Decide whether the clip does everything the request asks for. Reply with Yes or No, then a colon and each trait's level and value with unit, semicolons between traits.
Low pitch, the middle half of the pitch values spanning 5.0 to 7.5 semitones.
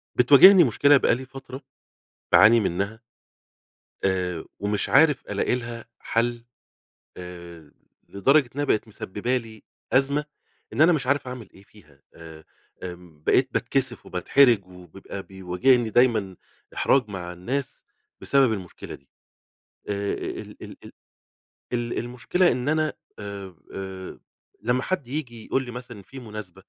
Yes: low, 115 Hz; wide, 5.5 semitones